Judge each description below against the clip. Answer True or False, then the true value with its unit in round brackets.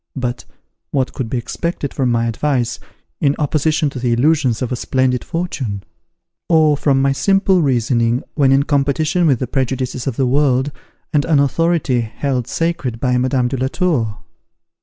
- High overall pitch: False (135 Hz)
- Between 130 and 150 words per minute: False (165 wpm)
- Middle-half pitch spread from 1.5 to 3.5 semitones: True (3.2 semitones)